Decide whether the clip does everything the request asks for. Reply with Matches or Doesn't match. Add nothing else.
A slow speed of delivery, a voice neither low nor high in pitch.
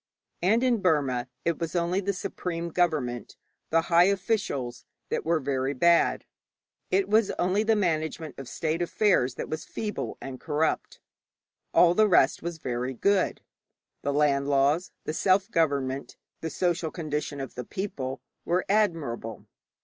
Doesn't match